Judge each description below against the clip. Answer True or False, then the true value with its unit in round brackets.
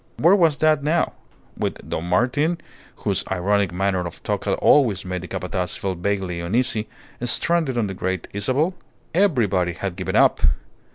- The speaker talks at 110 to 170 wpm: True (160 wpm)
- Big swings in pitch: True (7.6 semitones)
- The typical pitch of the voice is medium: False (100 Hz)